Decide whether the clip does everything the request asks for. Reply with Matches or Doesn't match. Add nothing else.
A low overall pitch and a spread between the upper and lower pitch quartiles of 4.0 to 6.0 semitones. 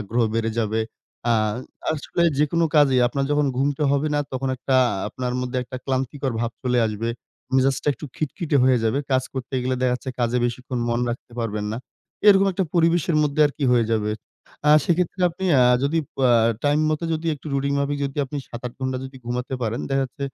Doesn't match